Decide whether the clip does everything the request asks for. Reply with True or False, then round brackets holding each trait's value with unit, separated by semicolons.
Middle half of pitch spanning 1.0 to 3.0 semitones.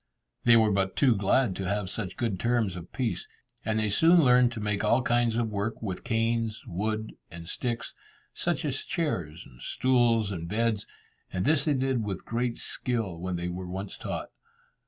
False (3.9 semitones)